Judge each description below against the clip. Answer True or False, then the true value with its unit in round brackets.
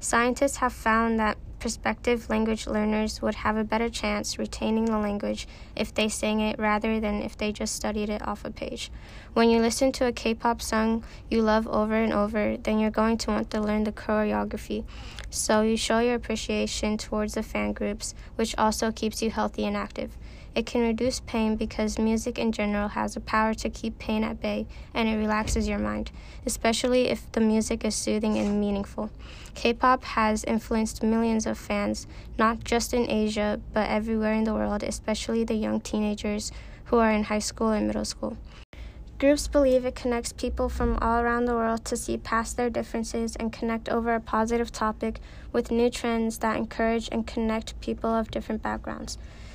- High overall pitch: True (220 Hz)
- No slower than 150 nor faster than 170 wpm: False (190 wpm)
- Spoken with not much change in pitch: True (1.4 semitones)